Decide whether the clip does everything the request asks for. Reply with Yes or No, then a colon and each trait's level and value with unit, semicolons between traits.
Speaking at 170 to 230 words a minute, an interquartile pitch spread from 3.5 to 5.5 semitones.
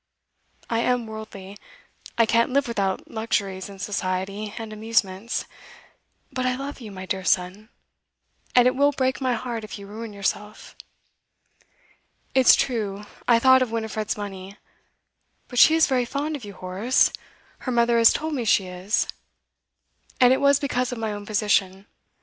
No: average, 160 wpm; average, 4.0 semitones